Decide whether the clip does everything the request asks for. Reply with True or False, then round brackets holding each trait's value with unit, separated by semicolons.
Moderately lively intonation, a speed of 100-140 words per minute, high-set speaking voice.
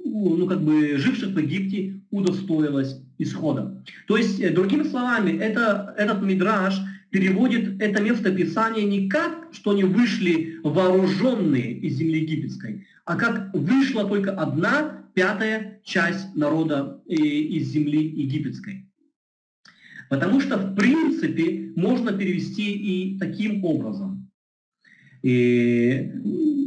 True (5.0 semitones; 110 wpm; 195 Hz)